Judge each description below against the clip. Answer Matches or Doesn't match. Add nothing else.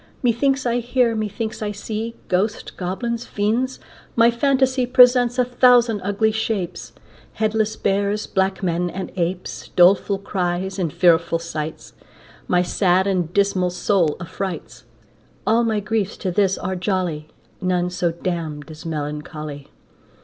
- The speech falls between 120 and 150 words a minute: Matches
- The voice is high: Matches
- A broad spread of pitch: Doesn't match